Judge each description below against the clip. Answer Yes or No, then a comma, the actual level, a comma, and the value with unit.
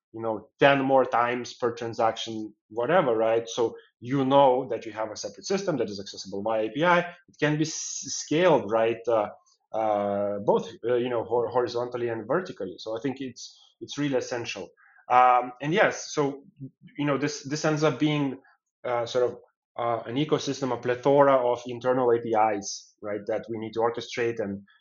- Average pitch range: Yes, average, 3.7 semitones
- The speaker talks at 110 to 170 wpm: No, average, 180 wpm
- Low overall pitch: Yes, low, 125 Hz